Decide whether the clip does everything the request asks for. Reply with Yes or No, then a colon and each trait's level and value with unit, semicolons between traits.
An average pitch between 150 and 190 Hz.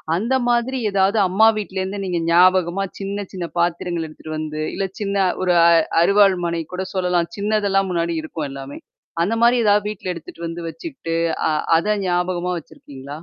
Yes: medium, 185 Hz